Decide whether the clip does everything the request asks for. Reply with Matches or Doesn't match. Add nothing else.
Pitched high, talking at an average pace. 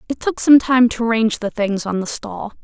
Doesn't match